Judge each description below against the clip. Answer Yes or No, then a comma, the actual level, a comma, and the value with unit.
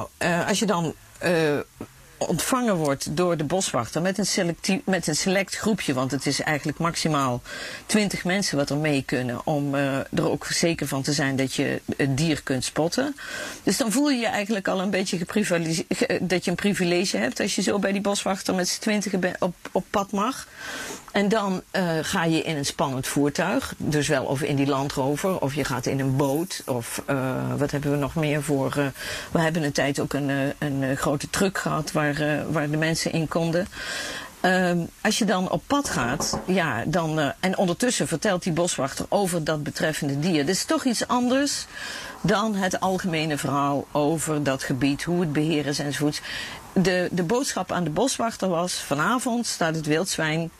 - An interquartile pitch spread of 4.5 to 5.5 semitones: Yes, average, 4.8 semitones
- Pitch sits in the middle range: Yes, medium, 165 Hz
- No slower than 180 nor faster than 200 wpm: Yes, average, 195 wpm